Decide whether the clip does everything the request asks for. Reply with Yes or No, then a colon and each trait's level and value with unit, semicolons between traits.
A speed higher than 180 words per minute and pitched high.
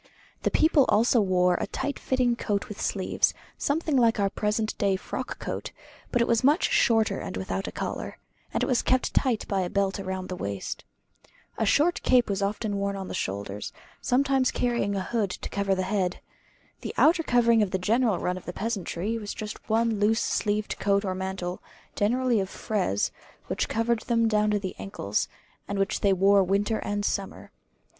Yes: average, 190 wpm; high, 210 Hz